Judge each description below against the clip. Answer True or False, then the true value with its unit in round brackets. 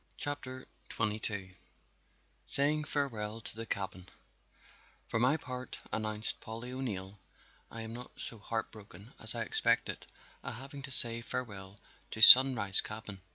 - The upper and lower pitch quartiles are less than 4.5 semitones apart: True (3.6 semitones)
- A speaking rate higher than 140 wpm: False (135 wpm)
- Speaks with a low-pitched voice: True (115 Hz)